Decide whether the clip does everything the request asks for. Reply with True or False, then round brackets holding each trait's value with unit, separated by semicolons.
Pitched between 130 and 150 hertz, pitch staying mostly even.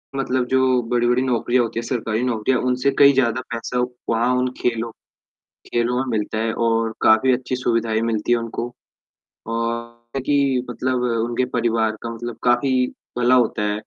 False (120 Hz; 1.7 semitones)